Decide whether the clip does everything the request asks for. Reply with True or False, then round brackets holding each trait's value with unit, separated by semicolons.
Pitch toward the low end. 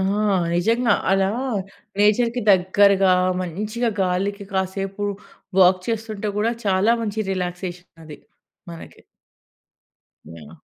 False (195 Hz)